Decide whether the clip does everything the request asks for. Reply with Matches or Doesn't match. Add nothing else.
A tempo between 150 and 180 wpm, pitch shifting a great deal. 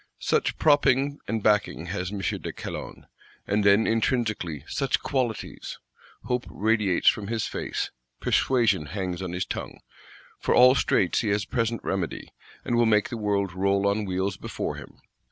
Doesn't match